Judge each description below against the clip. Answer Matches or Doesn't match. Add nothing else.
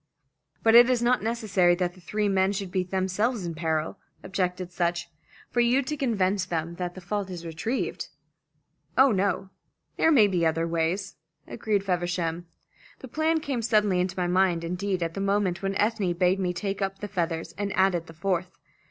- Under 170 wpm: Doesn't match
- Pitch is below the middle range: Doesn't match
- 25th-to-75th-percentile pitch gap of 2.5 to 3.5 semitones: Matches